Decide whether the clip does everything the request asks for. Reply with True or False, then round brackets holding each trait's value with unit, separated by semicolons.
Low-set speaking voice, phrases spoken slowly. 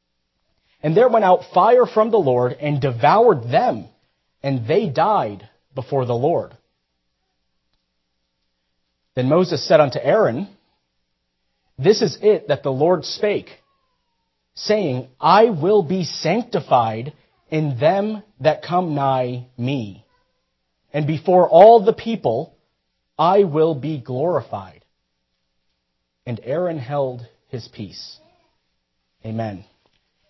True (130 Hz; 110 wpm)